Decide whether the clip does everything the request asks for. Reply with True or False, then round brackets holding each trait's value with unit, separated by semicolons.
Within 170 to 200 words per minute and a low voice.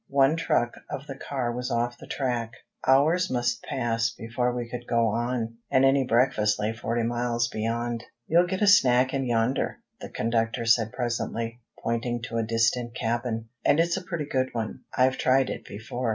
True (180 wpm; 120 Hz)